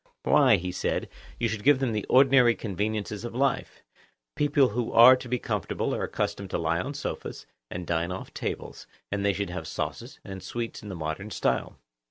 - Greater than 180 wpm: Yes, average, 195 wpm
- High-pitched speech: No, low, 105 Hz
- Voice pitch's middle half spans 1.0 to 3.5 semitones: No, average, 4.7 semitones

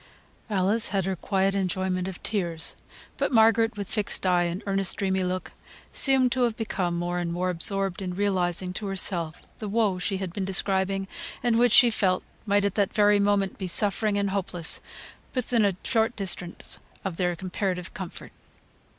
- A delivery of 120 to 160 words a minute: No, average, 170 wpm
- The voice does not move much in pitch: Yes, narrow, 2.3 semitones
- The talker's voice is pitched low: No, high, 195 Hz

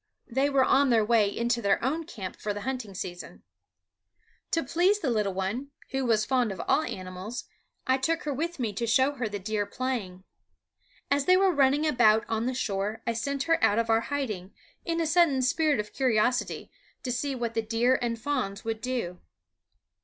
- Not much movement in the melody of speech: No, average, 4.6 semitones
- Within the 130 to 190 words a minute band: No, average, 200 wpm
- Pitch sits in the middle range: No, high, 240 Hz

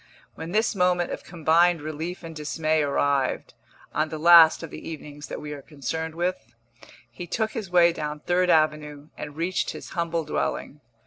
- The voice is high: No, medium, 160 Hz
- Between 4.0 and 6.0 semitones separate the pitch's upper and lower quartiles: No, narrow, 2.6 semitones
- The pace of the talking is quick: No, average, 175 wpm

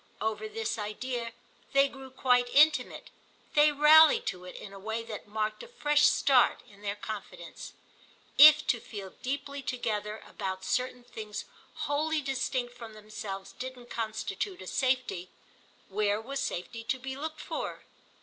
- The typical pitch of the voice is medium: No, high, 240 Hz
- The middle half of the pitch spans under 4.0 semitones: No, average, 4.5 semitones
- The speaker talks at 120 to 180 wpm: Yes, average, 150 wpm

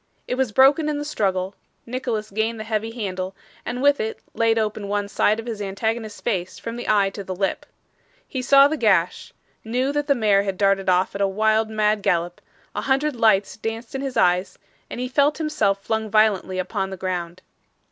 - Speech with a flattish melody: No, average, 4.0 semitones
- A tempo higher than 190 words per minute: Yes, average, 200 wpm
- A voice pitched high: Yes, high, 215 Hz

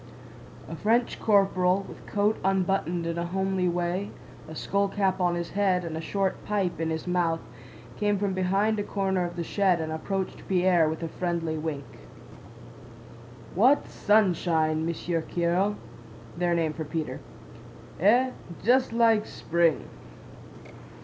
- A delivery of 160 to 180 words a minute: No, average, 140 wpm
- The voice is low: No, medium, 180 Hz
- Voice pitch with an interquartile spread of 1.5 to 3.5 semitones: Yes, average, 3.0 semitones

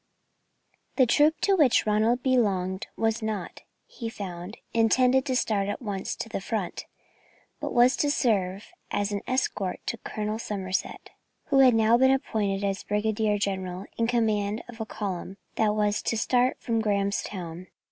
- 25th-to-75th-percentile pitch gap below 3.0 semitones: No, average, 3.3 semitones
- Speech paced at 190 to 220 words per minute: No, average, 155 wpm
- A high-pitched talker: Yes, high, 215 Hz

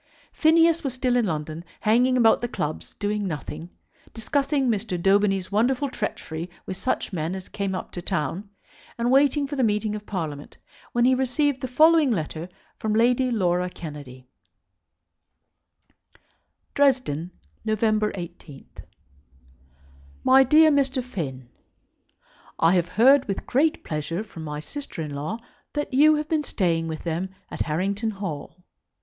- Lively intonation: Yes, wide, 7.3 semitones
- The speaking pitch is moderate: No, high, 210 Hz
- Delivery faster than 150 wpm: No, average, 145 wpm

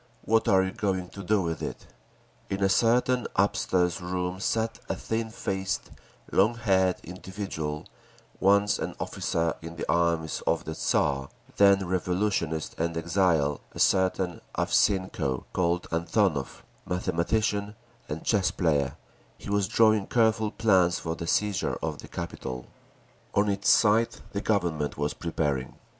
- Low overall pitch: Yes, very low, 95 Hz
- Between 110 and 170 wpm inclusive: Yes, average, 140 wpm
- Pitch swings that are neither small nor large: Yes, average, 3.6 semitones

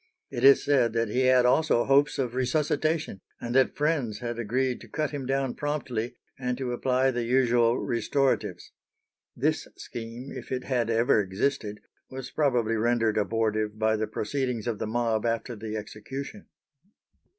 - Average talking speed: Yes, average, 160 wpm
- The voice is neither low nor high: No, low, 120 Hz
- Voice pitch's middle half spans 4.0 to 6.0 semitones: No, average, 2.8 semitones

